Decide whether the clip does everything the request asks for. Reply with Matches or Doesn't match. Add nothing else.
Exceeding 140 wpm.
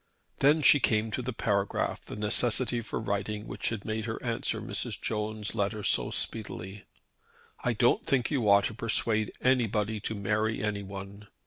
Matches